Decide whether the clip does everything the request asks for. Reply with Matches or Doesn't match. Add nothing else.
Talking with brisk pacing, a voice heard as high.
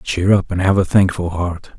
Doesn't match